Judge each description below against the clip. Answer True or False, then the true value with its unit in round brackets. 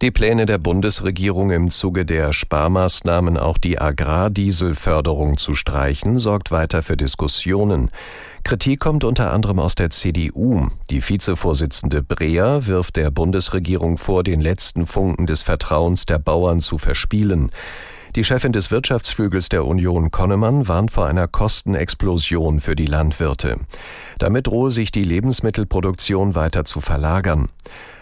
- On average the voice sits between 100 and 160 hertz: False (90 Hz)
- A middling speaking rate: True (135 wpm)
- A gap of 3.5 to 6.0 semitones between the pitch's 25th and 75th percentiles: True (4.0 semitones)